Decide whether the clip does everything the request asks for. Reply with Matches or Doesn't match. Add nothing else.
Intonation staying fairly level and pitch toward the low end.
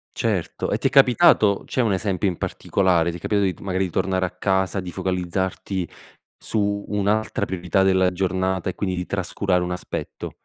Matches